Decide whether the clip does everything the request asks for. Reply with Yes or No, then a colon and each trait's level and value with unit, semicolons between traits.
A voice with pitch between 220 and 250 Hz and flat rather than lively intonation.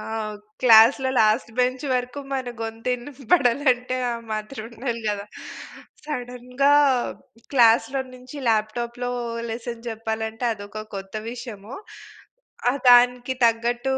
Yes: high, 240 Hz; narrow, 2.1 semitones